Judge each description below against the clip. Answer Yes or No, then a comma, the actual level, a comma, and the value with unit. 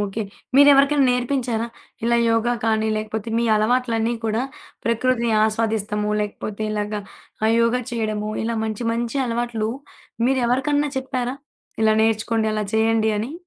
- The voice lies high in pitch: Yes, high, 230 Hz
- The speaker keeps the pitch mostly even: Yes, narrow, 2.2 semitones